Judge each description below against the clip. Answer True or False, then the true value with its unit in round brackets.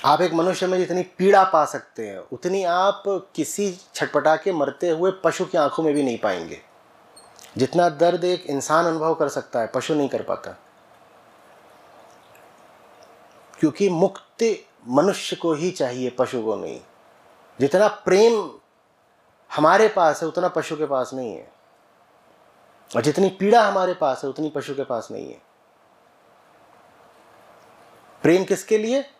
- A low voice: False (175 Hz)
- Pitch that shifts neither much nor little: True (4.5 semitones)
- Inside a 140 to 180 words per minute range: True (145 wpm)